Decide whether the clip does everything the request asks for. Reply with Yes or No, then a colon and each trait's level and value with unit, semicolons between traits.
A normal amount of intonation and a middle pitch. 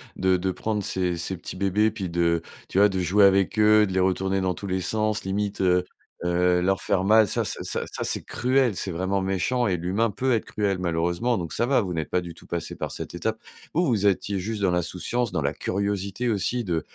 No: average, 3.0 semitones; very low, 95 Hz